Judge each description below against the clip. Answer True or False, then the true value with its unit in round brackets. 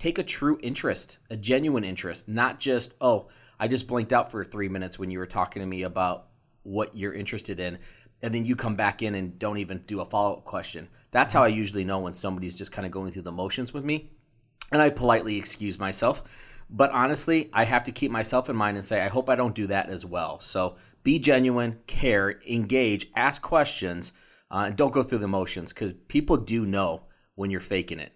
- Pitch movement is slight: False (4.5 semitones)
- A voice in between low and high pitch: False (105 Hz)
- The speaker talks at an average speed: False (220 wpm)